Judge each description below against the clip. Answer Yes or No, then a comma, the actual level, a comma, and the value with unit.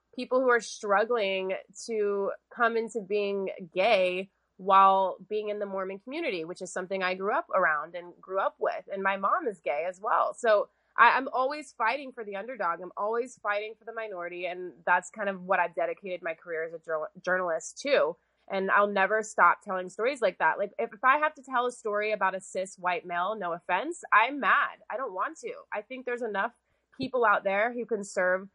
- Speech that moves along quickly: Yes, fast, 210 wpm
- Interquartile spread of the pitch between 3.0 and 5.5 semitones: Yes, average, 4.1 semitones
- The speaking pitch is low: No, high, 200 Hz